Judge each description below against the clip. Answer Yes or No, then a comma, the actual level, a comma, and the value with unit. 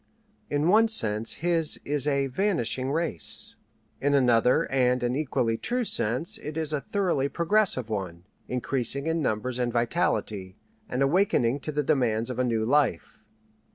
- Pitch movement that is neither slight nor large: Yes, average, 4.8 semitones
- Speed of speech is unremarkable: Yes, average, 155 wpm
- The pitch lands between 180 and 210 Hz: No, low, 135 Hz